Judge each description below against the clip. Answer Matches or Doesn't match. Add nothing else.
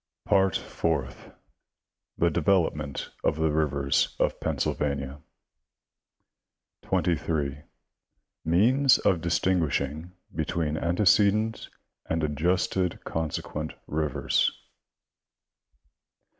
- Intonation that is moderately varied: Matches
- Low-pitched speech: Matches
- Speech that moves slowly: Matches